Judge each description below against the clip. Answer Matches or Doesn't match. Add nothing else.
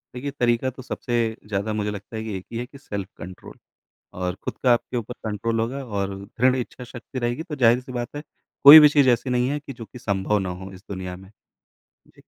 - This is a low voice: Matches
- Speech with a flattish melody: Doesn't match